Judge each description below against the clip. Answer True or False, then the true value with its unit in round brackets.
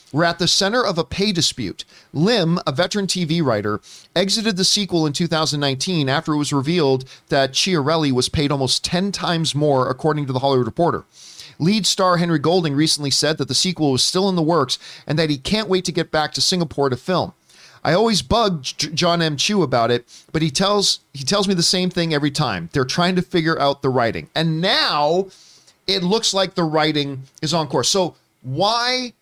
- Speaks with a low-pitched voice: False (160 Hz)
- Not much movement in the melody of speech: False (4.6 semitones)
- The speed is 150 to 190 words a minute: False (205 wpm)